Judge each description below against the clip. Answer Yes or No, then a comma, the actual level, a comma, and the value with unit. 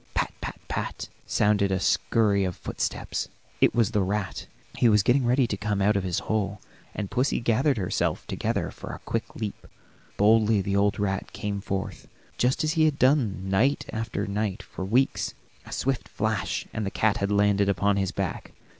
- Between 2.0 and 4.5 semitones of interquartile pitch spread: Yes, average, 2.7 semitones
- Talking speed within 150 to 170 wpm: No, average, 185 wpm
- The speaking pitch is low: Yes, low, 105 Hz